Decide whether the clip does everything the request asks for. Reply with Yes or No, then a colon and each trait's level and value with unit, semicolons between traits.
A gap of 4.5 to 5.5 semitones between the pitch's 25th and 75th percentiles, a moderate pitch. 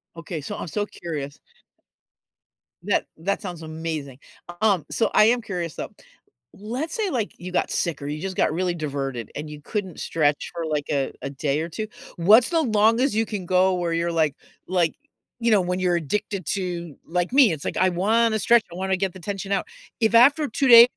Yes: average, 5.1 semitones; medium, 180 Hz